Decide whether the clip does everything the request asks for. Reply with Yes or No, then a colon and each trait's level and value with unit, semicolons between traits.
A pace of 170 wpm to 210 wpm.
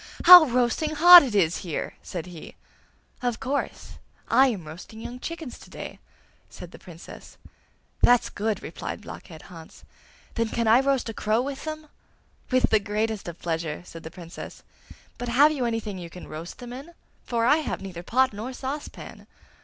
Yes: average, 175 wpm